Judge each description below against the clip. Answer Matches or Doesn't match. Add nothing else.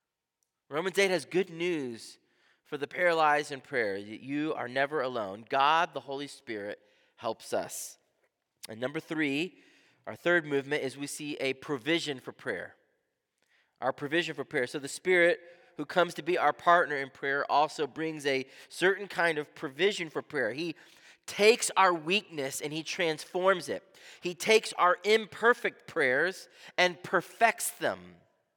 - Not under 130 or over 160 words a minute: Matches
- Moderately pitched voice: Matches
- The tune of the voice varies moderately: Matches